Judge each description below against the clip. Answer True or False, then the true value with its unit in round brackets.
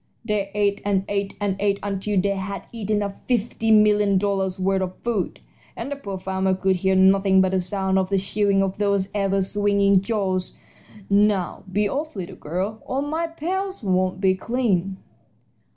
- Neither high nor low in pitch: False (200 Hz)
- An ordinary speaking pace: True (175 wpm)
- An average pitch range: False (1.7 semitones)